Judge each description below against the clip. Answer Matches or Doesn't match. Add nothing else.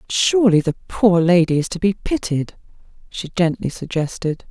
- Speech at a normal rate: Matches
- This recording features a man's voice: Doesn't match